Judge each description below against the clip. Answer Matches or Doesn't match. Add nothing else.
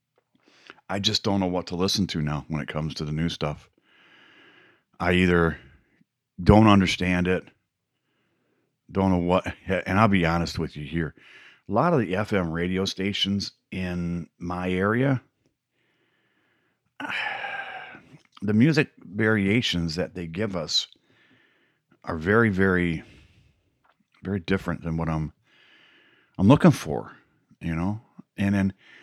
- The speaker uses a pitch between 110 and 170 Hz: Doesn't match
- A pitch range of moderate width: Matches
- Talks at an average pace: Doesn't match